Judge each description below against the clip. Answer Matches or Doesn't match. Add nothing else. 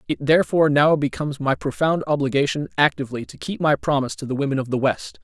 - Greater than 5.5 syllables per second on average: Matches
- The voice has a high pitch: Doesn't match